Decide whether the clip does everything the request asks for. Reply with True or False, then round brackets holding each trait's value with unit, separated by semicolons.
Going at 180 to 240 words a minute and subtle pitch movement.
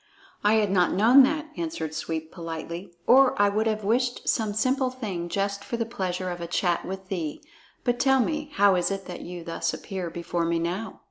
False (205 wpm; 5.4 semitones)